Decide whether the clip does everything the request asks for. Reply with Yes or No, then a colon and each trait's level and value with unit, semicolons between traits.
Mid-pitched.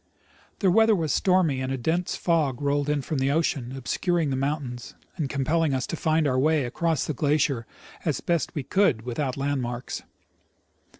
Yes: medium, 145 Hz